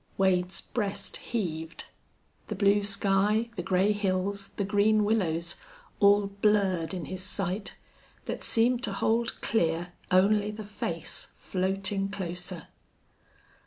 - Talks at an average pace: No, slow, 120 wpm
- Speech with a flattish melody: Yes, narrow, 2.2 semitones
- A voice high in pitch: Yes, high, 195 Hz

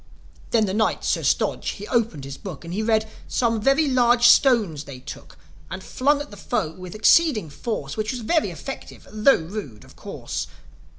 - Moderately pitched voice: No, high, 215 Hz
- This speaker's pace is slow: No, average, 185 wpm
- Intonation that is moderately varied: No, wide, 5.8 semitones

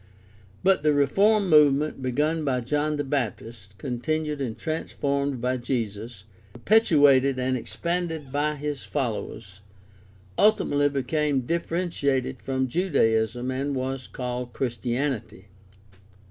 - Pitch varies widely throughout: No, average, 3.4 semitones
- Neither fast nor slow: No, slow, 110 wpm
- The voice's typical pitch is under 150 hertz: Yes, low, 135 Hz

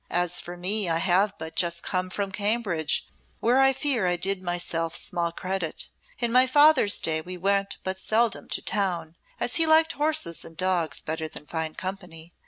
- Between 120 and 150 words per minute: No, average, 185 wpm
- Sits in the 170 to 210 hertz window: Yes, medium, 185 Hz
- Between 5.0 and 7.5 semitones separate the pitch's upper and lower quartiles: No, average, 4.2 semitones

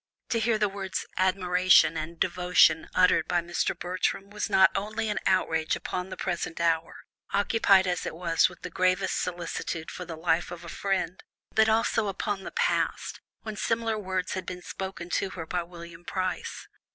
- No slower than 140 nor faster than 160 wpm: No, average, 175 wpm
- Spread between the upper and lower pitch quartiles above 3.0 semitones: No, narrow, 2.4 semitones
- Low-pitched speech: No, medium, 185 Hz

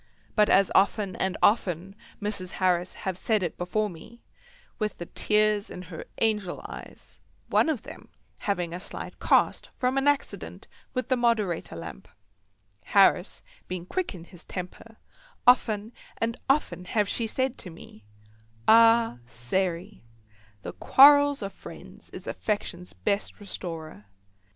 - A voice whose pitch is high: Yes, high, 200 Hz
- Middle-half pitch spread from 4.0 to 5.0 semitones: Yes, average, 4.3 semitones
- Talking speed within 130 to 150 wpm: Yes, slow, 135 wpm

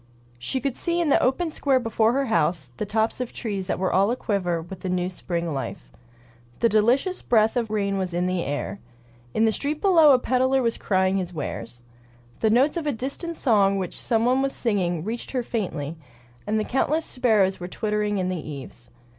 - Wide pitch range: Yes, wide, 5.7 semitones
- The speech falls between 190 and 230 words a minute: Yes, average, 200 wpm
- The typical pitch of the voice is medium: No, high, 215 Hz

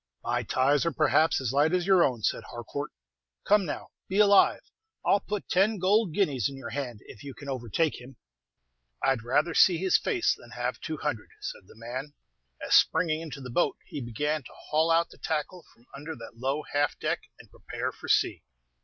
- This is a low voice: No, medium, 150 Hz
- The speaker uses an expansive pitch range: No, average, 4.8 semitones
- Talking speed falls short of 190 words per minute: No, average, 200 wpm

